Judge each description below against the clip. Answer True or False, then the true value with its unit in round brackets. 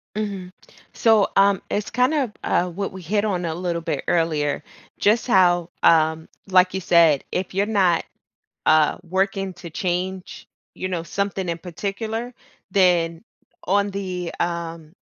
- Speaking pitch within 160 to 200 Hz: True (185 Hz)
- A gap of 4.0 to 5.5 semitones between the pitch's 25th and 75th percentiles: False (2.9 semitones)